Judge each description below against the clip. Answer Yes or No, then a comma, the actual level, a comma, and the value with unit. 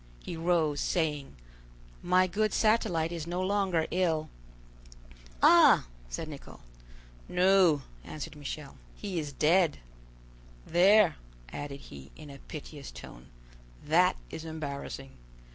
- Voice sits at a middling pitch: Yes, medium, 160 Hz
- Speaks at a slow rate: Yes, slow, 110 wpm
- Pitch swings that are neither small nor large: Yes, average, 3.9 semitones